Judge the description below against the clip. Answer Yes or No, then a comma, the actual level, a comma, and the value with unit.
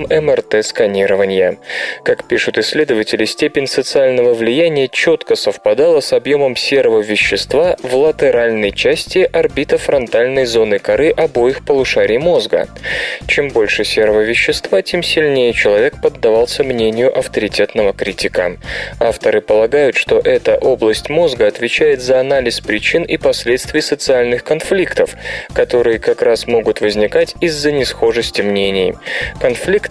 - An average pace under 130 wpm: Yes, average, 115 wpm